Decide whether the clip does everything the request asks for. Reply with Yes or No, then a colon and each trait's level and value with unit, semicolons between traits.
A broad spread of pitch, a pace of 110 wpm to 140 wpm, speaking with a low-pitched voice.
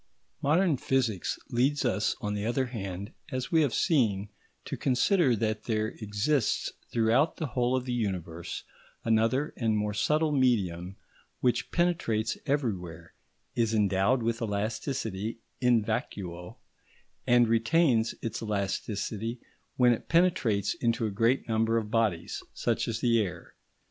No: average, 3.7 semitones; slow, 135 wpm; low, 115 Hz